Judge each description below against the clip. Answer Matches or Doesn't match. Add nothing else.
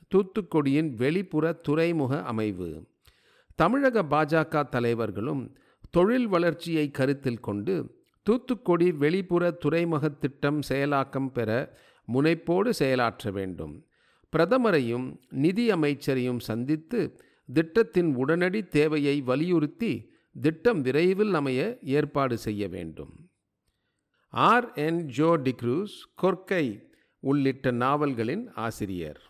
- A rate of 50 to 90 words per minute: Matches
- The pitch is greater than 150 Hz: Doesn't match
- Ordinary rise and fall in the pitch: Matches